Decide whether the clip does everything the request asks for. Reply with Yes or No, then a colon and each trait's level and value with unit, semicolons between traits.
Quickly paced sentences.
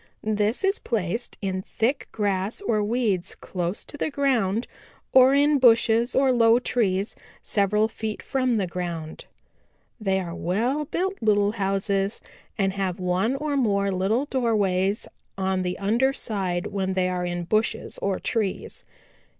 No: average, 145 wpm